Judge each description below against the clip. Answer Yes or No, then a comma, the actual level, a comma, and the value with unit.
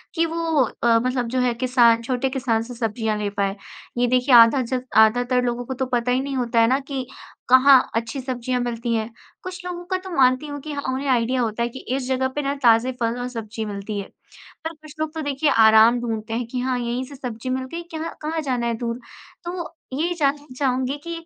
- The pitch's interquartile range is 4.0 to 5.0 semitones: No, average, 3.2 semitones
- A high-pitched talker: Yes, very high, 255 Hz